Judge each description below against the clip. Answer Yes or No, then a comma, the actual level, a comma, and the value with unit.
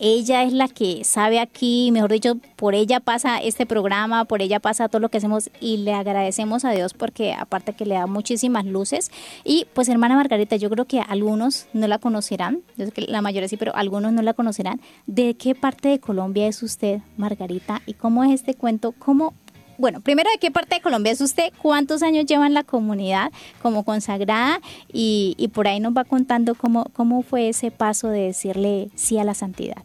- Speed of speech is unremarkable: No, fast, 205 wpm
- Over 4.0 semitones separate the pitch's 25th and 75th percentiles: No, average, 3.2 semitones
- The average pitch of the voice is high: Yes, high, 225 Hz